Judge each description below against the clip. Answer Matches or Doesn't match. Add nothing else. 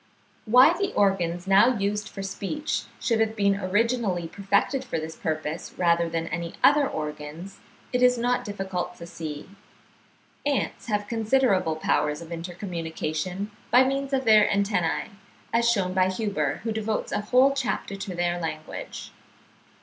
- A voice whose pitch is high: Matches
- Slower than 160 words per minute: Matches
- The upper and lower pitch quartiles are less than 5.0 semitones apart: Doesn't match